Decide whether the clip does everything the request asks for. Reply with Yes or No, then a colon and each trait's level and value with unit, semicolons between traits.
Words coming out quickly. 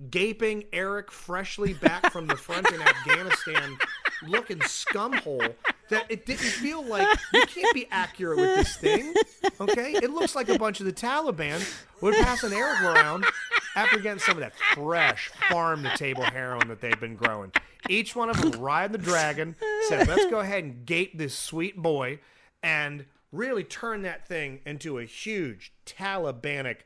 No: average, 165 wpm